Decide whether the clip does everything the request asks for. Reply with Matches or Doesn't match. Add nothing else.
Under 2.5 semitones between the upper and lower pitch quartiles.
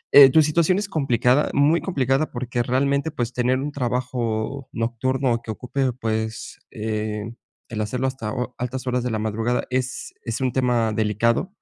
Doesn't match